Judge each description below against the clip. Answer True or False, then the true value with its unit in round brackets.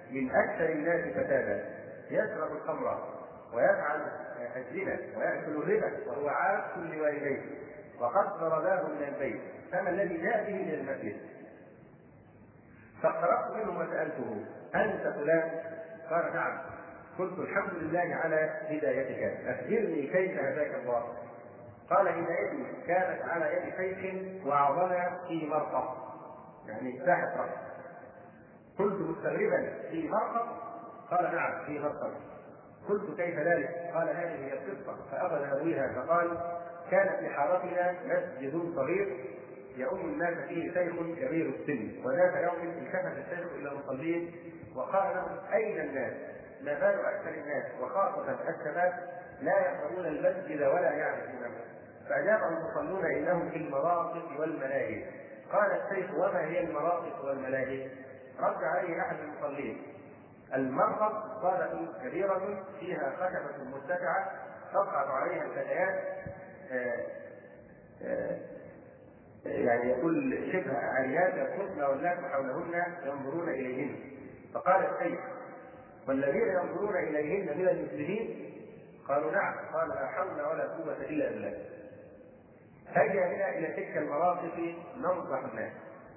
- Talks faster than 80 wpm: True (110 wpm)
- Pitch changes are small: False (4.2 semitones)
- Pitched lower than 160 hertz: False (170 Hz)